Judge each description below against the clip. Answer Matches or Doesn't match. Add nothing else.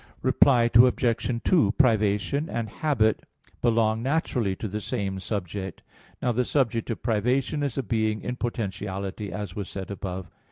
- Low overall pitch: Matches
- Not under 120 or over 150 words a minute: Doesn't match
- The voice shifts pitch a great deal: Doesn't match